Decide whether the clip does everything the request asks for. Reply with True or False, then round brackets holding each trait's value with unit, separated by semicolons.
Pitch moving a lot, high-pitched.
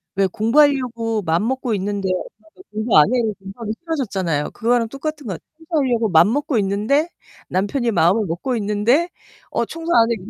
False (4.9 semitones; 225 Hz)